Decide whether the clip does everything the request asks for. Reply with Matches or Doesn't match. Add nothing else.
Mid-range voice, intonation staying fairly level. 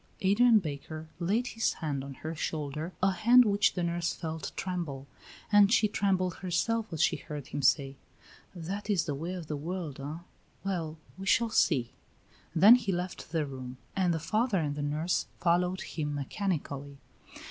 Doesn't match